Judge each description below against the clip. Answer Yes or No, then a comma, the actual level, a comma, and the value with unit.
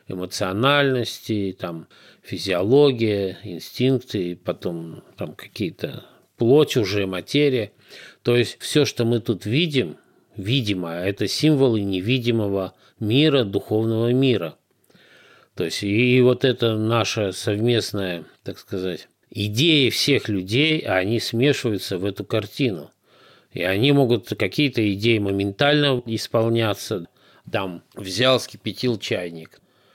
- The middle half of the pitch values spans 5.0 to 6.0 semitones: No, average, 4.5 semitones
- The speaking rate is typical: No, slow, 105 wpm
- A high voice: No, low, 110 Hz